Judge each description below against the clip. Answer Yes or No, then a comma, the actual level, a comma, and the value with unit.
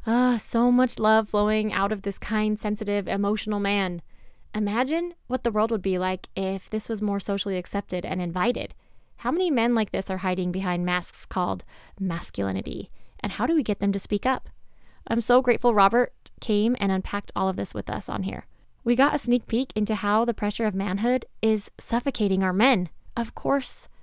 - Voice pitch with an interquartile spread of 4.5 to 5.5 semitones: No, average, 3.5 semitones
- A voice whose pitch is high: Yes, high, 215 Hz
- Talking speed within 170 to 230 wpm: Yes, average, 195 wpm